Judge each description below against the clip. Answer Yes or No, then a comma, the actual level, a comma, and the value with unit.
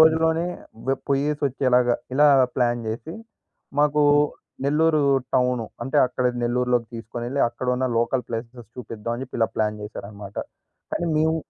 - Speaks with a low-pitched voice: Yes, low, 125 Hz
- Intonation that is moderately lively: Yes, average, 4.0 semitones